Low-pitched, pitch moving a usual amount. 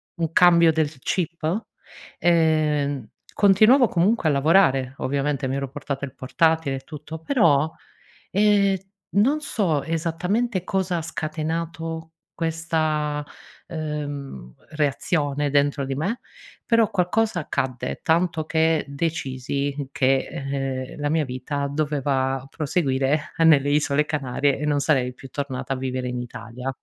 No: medium, 150 Hz; average, 3.3 semitones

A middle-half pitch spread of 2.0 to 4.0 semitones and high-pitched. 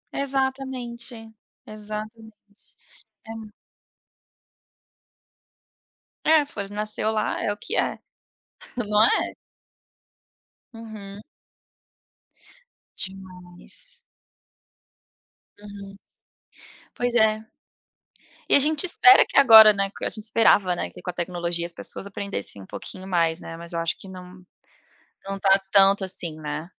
Yes: average, 3.6 semitones; high, 205 Hz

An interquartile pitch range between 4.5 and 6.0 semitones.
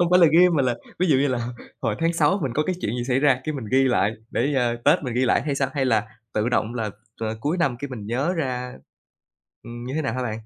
No: average, 3.7 semitones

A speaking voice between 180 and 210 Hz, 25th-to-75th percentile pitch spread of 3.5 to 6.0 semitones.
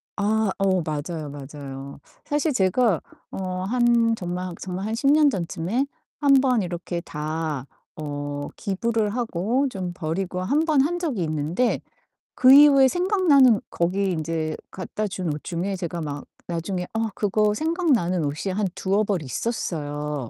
No: high, 190 Hz; wide, 6.5 semitones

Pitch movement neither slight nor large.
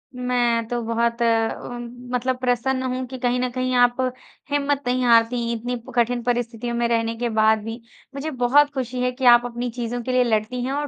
No: narrow, 1.4 semitones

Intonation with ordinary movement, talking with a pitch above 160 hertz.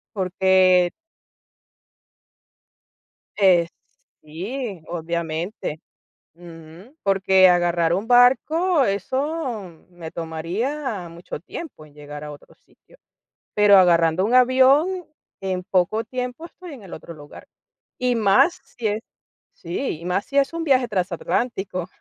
No: wide, 6.6 semitones; high, 190 Hz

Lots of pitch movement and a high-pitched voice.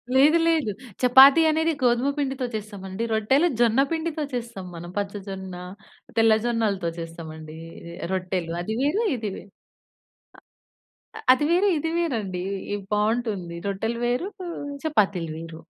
Yes: wide, 6.2 semitones; high, 220 Hz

